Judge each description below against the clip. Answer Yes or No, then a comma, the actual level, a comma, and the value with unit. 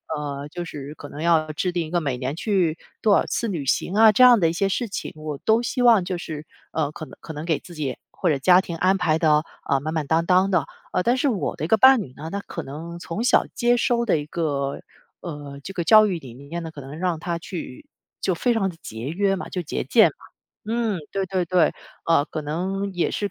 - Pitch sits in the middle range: Yes, medium, 170 Hz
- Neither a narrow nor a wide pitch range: Yes, average, 4.3 semitones